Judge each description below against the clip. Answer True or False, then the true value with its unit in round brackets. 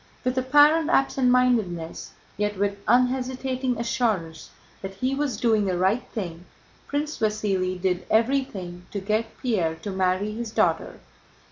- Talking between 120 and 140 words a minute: True (135 wpm)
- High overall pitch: True (215 Hz)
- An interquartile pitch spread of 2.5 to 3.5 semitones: False (5.0 semitones)